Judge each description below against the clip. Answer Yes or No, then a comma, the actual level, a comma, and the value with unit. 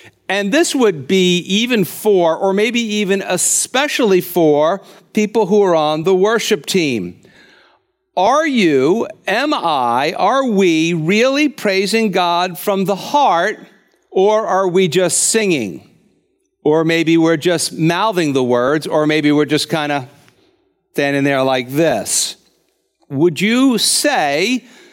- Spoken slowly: Yes, slow, 130 wpm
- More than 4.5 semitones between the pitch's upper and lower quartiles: Yes, average, 5.2 semitones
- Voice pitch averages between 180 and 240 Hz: Yes, high, 190 Hz